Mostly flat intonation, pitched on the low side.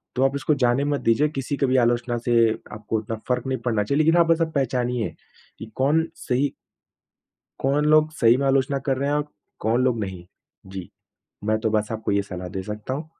No: average, 4.1 semitones; low, 125 Hz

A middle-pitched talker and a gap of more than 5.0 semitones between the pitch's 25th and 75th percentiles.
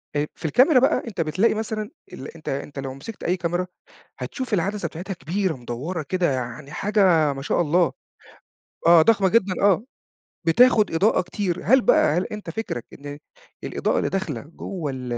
Yes: medium, 175 Hz; wide, 5.6 semitones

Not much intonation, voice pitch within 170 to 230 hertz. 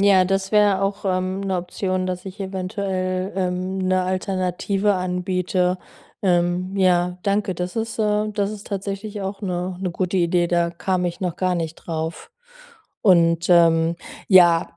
Yes: narrow, 1.6 semitones; medium, 185 Hz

